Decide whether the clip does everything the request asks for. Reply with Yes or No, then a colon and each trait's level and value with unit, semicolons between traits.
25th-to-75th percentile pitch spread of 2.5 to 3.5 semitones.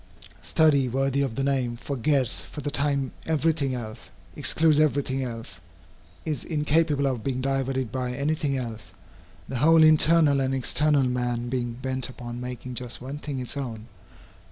Yes: average, 2.8 semitones